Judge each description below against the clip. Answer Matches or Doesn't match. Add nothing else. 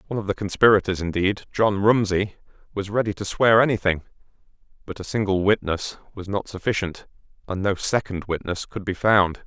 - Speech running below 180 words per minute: Matches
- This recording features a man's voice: Matches